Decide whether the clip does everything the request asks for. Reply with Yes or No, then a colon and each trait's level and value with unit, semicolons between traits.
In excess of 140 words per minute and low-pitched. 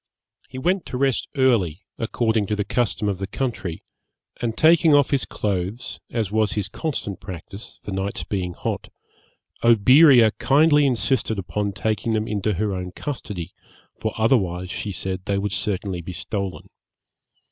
Yes: average, 155 wpm; low, 105 Hz